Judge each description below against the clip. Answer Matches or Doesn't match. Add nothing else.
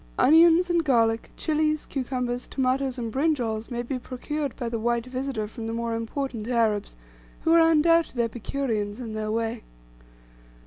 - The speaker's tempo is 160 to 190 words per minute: Doesn't match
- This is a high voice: Matches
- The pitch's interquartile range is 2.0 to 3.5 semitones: Doesn't match